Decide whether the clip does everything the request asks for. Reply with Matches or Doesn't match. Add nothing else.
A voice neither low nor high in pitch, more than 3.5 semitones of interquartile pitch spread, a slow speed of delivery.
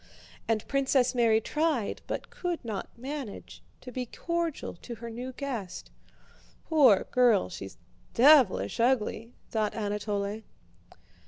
Doesn't match